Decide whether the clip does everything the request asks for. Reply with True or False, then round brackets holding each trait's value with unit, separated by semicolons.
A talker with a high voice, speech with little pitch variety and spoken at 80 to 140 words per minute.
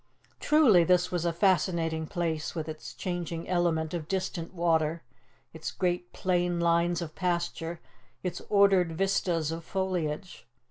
False (175 Hz; 1.9 semitones; 135 wpm)